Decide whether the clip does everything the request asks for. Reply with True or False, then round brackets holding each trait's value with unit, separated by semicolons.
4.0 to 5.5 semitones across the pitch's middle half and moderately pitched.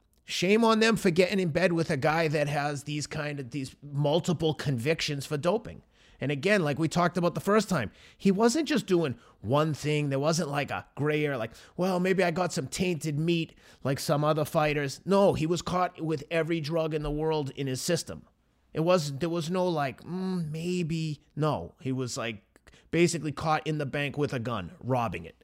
False (3.6 semitones; 155 Hz)